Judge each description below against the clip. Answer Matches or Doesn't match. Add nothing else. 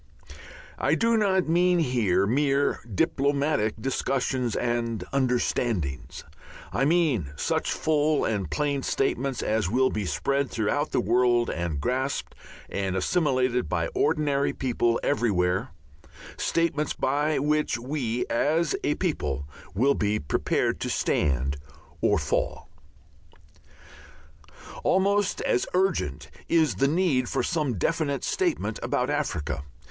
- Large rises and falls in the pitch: Matches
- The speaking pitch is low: Matches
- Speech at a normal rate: Doesn't match